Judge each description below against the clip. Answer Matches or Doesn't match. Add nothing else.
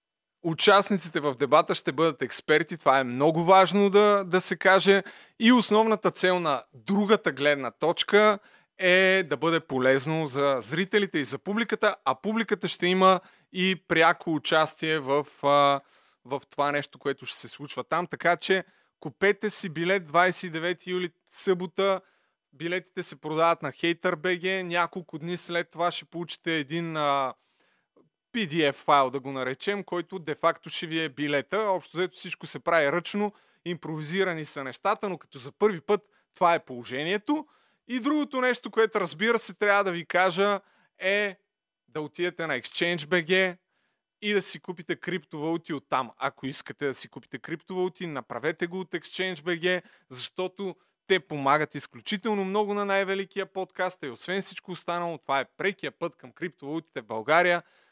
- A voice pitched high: Doesn't match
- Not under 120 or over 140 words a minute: Doesn't match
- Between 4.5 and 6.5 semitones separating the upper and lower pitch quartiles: Doesn't match